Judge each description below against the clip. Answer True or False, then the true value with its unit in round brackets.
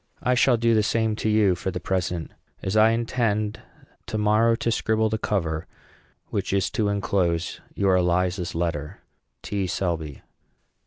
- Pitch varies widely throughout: False (3.8 semitones)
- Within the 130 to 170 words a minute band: True (155 wpm)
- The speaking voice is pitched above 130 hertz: False (100 Hz)